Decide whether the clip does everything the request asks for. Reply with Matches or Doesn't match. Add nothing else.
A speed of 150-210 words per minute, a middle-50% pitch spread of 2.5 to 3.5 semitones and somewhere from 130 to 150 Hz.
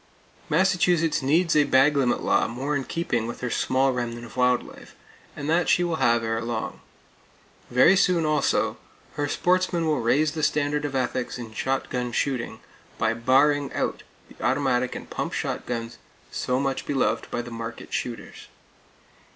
Doesn't match